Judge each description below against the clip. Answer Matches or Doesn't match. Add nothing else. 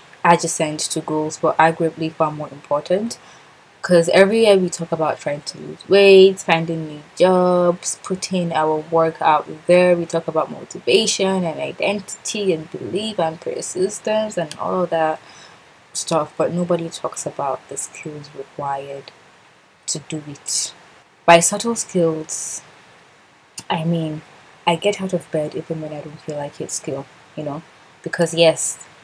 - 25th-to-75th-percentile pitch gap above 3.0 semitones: Doesn't match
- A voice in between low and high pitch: Matches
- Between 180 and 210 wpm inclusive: Doesn't match